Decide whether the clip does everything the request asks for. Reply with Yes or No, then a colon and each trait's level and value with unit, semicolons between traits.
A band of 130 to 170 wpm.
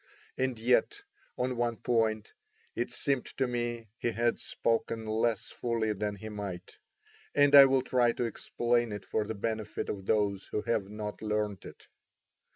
Yes: average, 165 wpm